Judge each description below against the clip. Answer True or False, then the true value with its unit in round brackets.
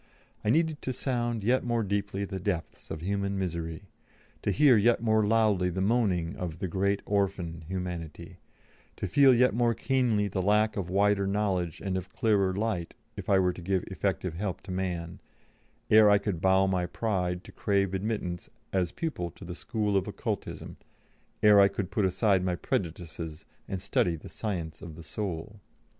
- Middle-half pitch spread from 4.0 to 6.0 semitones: False (3.0 semitones)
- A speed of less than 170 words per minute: False (180 wpm)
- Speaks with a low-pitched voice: True (95 Hz)